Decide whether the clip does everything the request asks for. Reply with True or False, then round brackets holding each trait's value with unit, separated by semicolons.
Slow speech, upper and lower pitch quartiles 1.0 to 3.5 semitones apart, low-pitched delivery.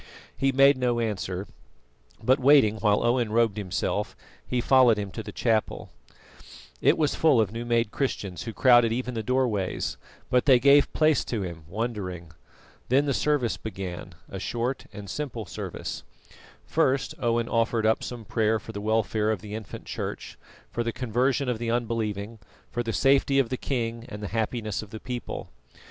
False (175 wpm; 3.0 semitones; 115 Hz)